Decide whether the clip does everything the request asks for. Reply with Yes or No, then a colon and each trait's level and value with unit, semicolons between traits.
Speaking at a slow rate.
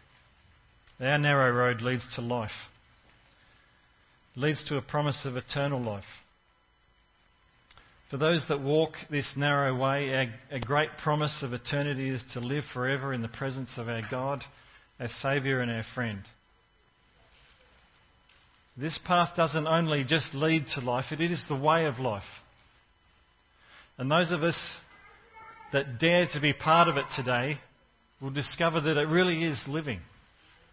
No: average, 145 wpm